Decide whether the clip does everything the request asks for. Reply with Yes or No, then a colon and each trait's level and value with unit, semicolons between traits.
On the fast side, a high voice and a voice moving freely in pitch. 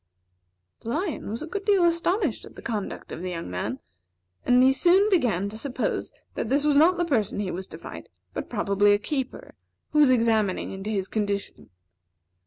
No: average, 195 wpm; high, 240 Hz; wide, 7.5 semitones